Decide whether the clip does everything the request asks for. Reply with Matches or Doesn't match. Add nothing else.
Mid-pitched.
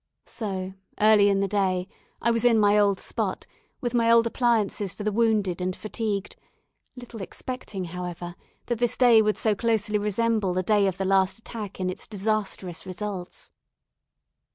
Doesn't match